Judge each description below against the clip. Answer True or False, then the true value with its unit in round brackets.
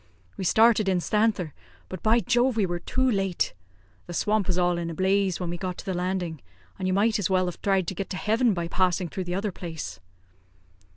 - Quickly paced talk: True (220 wpm)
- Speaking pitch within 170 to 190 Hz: True (185 Hz)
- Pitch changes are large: False (3.0 semitones)